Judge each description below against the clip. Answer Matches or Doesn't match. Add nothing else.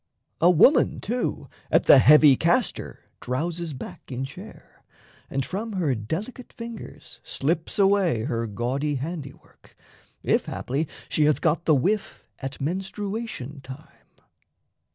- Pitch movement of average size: Doesn't match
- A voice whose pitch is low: Doesn't match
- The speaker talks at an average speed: Doesn't match